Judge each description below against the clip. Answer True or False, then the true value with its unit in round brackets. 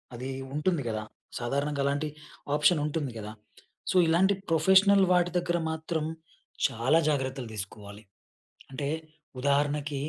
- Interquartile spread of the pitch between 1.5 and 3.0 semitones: False (3.7 semitones)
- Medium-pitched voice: True (145 Hz)